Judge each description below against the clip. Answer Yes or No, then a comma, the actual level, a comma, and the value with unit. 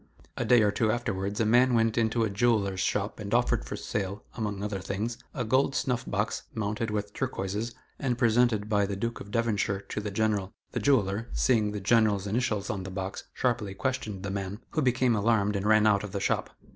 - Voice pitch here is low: Yes, low, 105 Hz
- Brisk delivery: Yes, fast, 210 wpm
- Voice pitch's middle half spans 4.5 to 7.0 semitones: No, average, 2.7 semitones